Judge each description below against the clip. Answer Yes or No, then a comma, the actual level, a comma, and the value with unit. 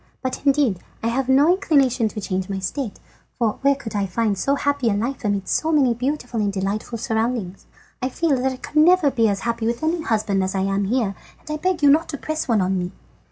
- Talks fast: Yes, fast, 235 wpm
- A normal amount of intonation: No, wide, 5.7 semitones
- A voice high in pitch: Yes, high, 235 Hz